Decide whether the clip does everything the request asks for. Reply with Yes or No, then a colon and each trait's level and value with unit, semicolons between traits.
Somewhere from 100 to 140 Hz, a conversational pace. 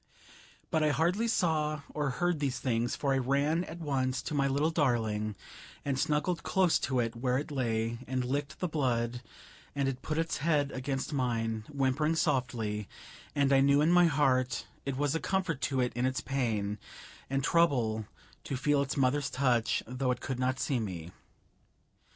Yes: low, 135 Hz; average, 180 wpm